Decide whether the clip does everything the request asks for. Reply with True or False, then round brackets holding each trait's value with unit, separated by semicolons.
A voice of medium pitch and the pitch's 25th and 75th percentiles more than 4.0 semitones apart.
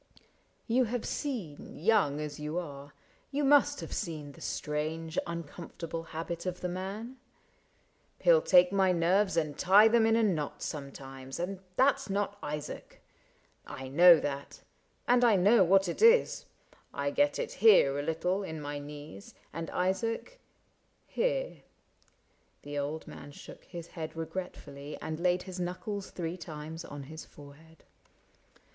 True (170 Hz; 5.1 semitones)